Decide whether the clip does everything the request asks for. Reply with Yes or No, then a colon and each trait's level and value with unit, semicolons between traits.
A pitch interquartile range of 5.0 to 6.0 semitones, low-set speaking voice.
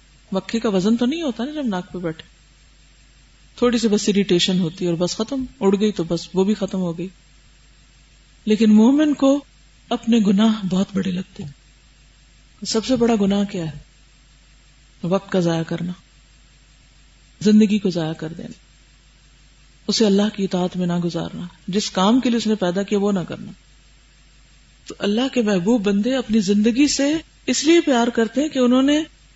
No: average, 5.3 semitones; high, 200 Hz